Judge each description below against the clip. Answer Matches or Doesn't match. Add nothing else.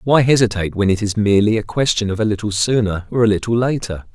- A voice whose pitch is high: Doesn't match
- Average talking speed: Doesn't match